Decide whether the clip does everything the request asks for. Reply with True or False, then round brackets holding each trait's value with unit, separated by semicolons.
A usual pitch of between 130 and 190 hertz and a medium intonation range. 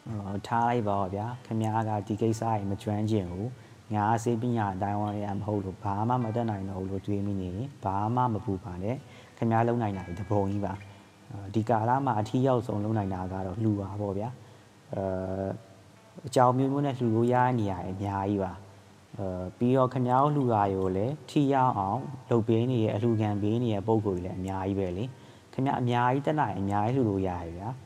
False (105 Hz; 3.6 semitones)